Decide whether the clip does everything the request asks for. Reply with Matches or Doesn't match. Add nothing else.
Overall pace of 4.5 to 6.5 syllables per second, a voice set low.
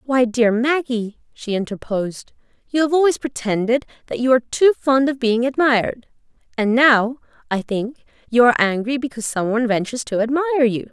Doesn't match